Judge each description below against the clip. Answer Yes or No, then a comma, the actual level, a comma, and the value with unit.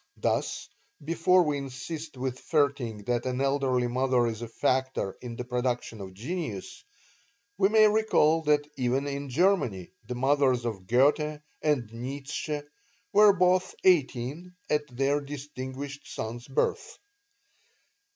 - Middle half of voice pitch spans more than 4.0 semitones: No, average, 3.6 semitones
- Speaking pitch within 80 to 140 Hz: Yes, low, 135 Hz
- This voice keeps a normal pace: No, slow, 130 wpm